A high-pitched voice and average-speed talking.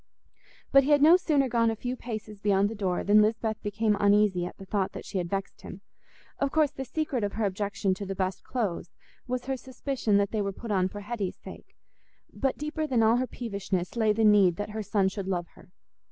No: high, 210 Hz; fast, 225 wpm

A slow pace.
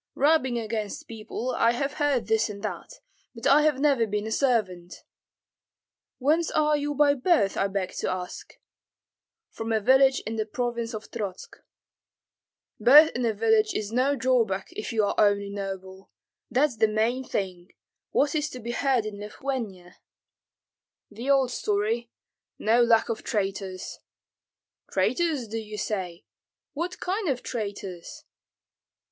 No: average, 145 wpm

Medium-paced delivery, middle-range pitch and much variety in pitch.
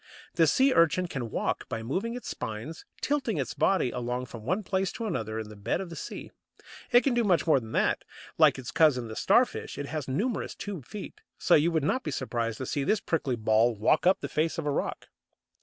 No: fast, 225 wpm; medium, 155 Hz; wide, 8.1 semitones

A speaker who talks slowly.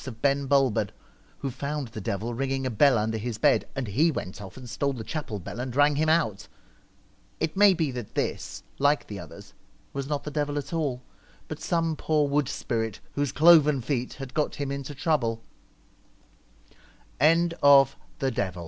No: average, 165 wpm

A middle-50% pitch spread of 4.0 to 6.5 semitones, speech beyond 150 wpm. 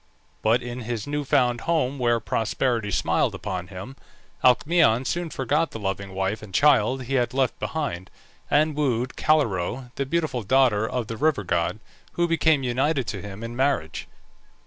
Yes: average, 4.8 semitones; average, 165 wpm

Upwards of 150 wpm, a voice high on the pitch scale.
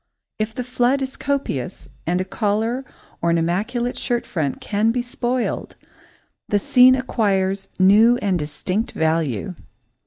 No: slow, 135 wpm; high, 210 Hz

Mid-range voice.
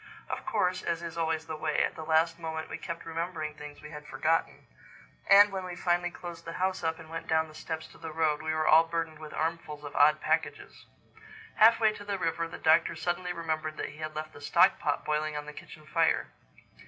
Yes: medium, 160 Hz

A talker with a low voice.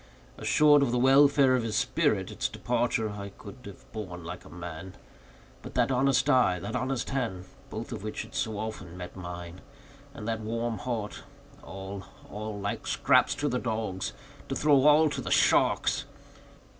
Yes: low, 110 Hz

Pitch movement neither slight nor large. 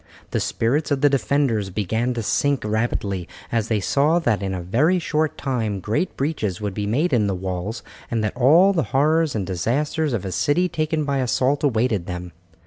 No: wide, 6.1 semitones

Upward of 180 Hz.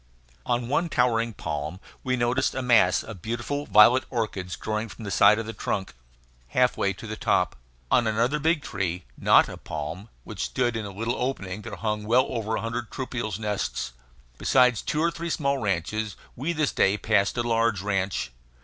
No: low, 115 Hz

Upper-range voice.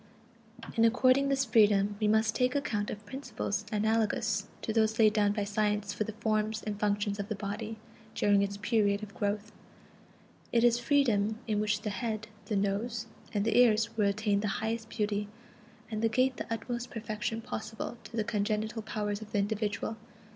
Yes: high, 215 Hz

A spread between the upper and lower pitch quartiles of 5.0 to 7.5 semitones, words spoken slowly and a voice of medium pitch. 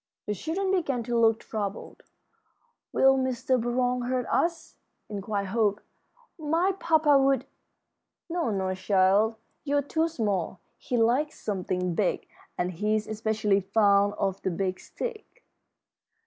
No: wide, 5.5 semitones; slow, 130 wpm; high, 225 Hz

